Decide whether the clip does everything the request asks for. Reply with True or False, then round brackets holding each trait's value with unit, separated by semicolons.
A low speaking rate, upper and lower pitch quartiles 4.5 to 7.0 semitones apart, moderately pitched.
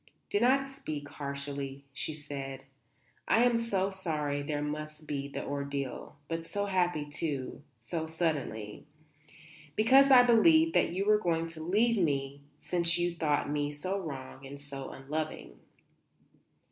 False (145 wpm; 5.2 semitones; 155 Hz)